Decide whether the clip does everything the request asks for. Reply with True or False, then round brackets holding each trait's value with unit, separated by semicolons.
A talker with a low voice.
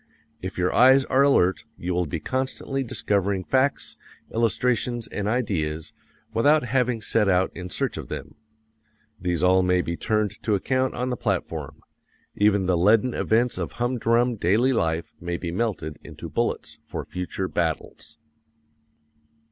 True (105 Hz)